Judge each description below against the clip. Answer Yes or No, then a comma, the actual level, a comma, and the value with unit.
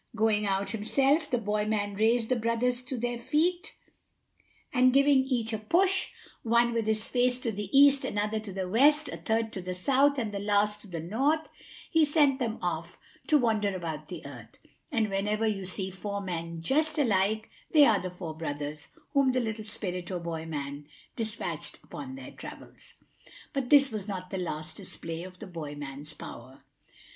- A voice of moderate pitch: No, high, 215 Hz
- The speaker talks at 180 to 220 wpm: Yes, average, 185 wpm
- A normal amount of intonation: No, wide, 5.7 semitones